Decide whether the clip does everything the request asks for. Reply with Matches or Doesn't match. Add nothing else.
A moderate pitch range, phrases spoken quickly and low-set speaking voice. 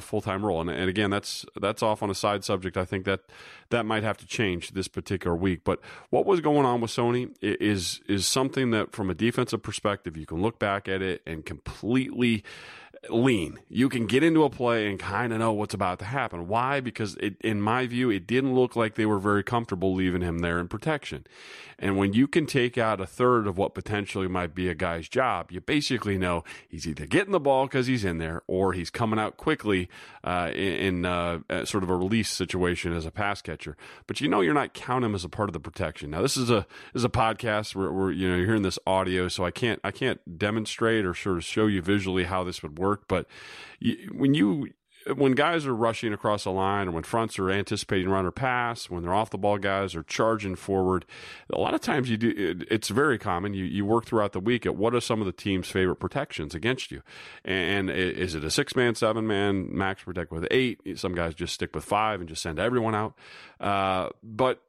Matches